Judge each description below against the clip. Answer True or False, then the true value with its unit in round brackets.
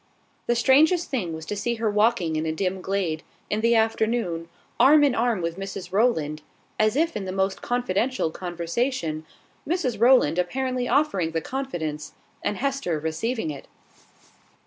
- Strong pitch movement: True (6.9 semitones)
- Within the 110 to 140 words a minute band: False (155 wpm)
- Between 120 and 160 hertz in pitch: False (210 Hz)